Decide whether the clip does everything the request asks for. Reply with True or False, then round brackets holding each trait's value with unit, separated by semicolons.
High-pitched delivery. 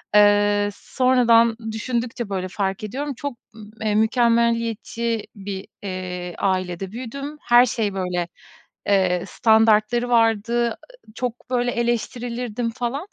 True (225 Hz)